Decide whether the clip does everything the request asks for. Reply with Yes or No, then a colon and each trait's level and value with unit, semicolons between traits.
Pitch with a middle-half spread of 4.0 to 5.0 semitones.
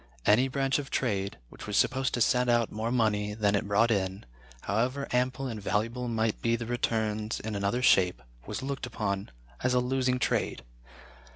No: average, 3.3 semitones